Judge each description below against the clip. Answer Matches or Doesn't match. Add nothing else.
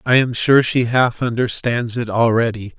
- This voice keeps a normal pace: Matches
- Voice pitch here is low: Matches